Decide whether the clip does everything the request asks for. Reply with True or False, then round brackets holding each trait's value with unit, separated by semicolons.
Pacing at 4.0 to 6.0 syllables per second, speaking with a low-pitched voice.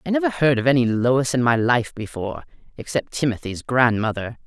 True (5.5 syllables/s; 130 Hz)